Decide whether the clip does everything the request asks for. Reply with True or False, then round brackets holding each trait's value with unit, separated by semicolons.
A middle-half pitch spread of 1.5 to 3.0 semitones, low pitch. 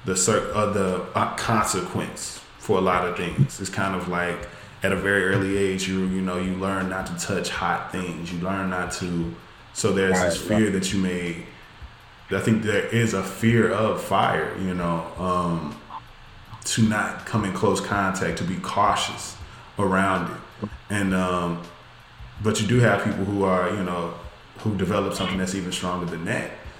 True (2.4 semitones; 95 Hz)